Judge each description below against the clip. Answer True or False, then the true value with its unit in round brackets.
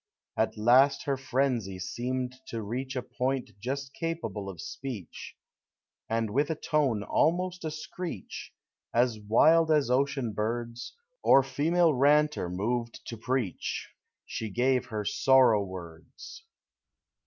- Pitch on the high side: False (125 Hz)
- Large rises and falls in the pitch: False (4.3 semitones)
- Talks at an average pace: False (130 wpm)